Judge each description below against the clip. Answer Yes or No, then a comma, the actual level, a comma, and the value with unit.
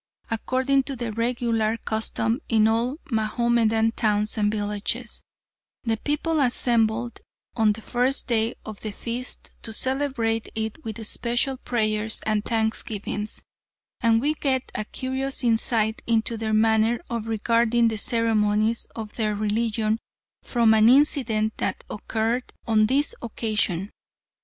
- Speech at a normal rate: No, slow, 130 wpm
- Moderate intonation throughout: No, narrow, 1.9 semitones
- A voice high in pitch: Yes, high, 225 Hz